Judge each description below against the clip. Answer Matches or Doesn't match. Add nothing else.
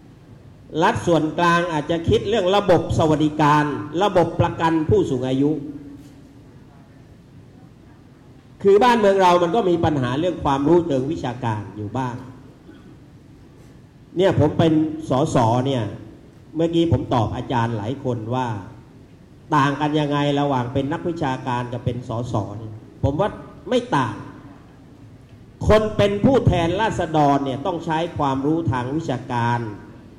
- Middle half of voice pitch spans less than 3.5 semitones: Doesn't match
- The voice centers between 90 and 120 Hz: Doesn't match